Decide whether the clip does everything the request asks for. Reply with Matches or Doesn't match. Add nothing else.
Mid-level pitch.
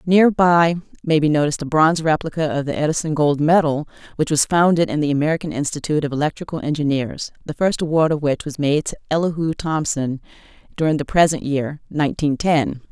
Matches